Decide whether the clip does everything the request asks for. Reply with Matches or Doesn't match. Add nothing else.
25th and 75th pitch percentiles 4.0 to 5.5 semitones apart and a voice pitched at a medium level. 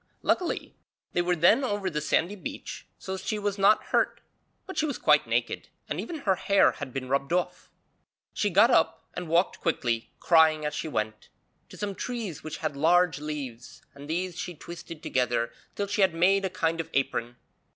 Matches